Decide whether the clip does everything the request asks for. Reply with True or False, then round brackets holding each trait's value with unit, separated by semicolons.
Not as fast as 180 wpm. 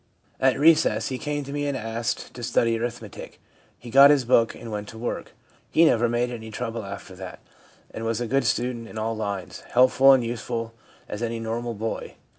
False (200 wpm)